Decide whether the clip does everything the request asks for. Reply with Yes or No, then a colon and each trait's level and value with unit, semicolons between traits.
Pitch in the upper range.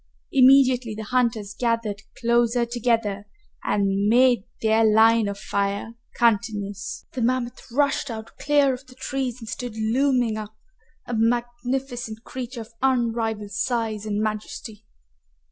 Yes: high, 230 Hz